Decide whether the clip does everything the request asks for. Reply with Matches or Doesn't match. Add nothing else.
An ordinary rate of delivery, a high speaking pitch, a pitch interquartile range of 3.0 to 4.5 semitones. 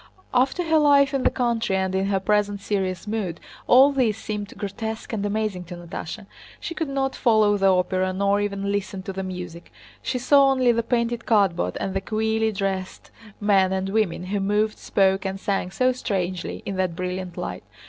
Matches